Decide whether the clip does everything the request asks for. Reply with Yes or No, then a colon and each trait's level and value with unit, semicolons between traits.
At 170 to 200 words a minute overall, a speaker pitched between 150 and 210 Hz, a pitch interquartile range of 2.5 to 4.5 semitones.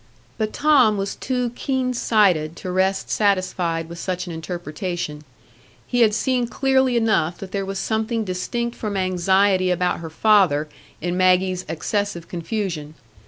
No: average, 145 wpm; high, 190 Hz; average, 4.0 semitones